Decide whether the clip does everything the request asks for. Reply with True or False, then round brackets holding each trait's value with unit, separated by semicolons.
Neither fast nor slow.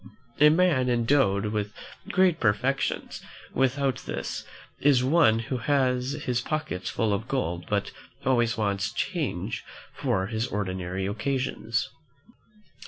False (120 wpm)